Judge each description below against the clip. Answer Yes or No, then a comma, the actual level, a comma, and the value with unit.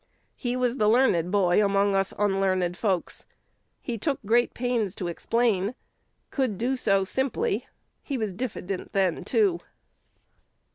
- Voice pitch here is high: Yes, high, 210 Hz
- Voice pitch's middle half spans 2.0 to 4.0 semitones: No, average, 4.4 semitones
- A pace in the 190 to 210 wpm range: No, average, 140 wpm